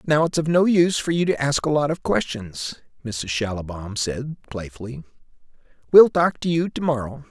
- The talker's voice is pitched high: No, low, 135 Hz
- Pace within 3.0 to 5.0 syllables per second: No, 5.2 syllables/s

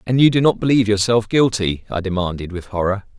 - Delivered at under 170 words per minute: No, fast, 205 wpm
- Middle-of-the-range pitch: No, low, 105 Hz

